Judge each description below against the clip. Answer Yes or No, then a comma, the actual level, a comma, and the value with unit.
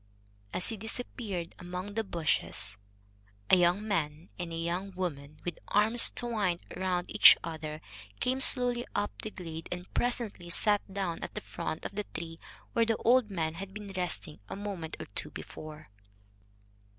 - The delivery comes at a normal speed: Yes, average, 160 wpm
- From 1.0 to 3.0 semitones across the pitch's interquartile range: No, average, 4.2 semitones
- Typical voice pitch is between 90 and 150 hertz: No, medium, 185 Hz